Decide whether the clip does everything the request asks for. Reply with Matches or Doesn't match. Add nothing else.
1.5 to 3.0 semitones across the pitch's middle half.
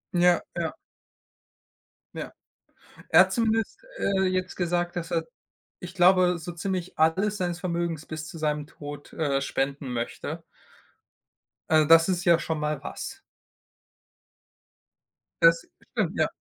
Matches